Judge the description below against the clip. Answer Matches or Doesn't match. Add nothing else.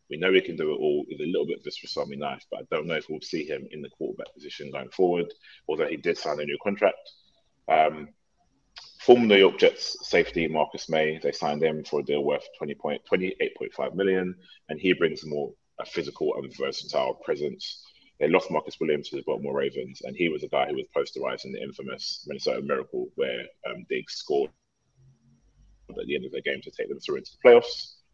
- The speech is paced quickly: Matches